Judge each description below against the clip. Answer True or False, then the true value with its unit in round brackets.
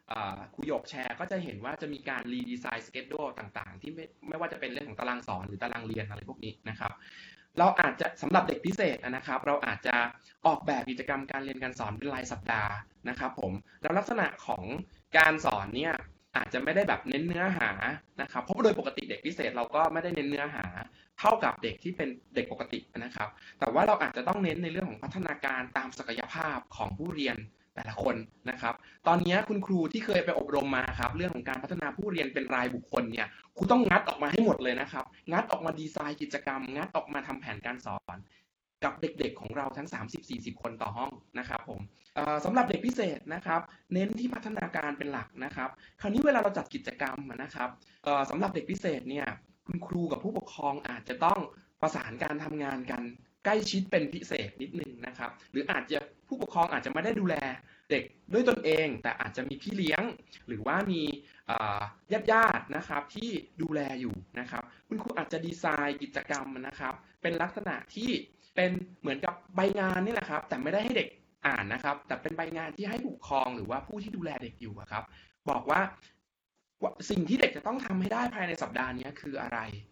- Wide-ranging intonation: True (6.5 semitones)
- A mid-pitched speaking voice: True (145 Hz)